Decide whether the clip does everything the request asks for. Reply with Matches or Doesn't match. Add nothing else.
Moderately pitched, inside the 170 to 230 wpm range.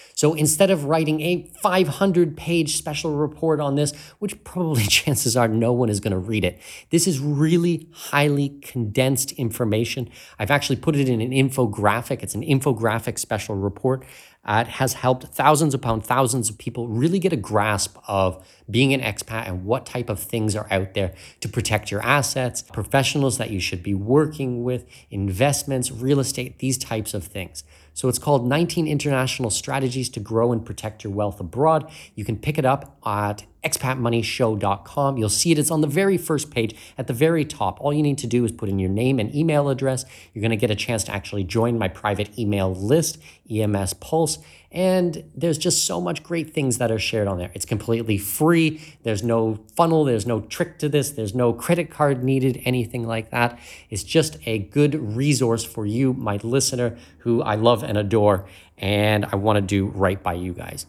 Doesn't match